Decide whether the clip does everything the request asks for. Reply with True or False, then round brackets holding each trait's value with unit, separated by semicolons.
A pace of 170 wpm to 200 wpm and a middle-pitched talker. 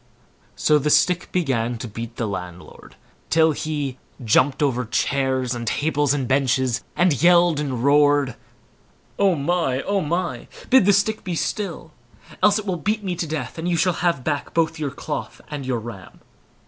True (175 wpm; 145 Hz)